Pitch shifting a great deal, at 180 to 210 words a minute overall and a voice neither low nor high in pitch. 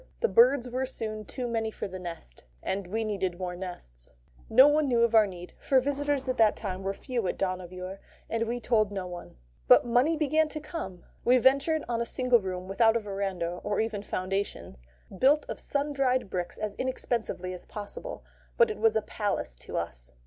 No: wide, 5.8 semitones; average, 200 wpm; high, 220 Hz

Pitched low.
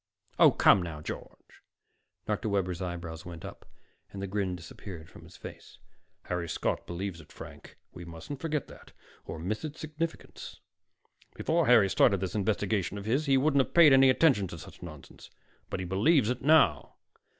Yes: low, 100 Hz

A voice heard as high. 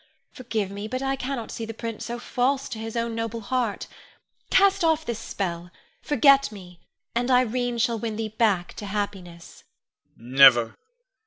Yes: high, 225 Hz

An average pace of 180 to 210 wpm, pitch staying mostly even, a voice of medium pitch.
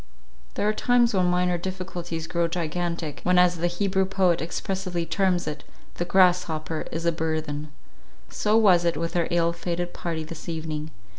No: average, 170 wpm; narrow, 2.0 semitones; medium, 175 Hz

